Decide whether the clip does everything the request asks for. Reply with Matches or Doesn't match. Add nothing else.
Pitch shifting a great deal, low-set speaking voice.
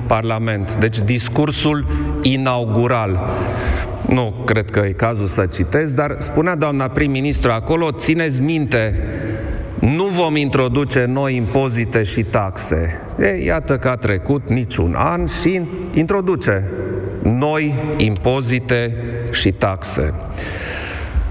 Matches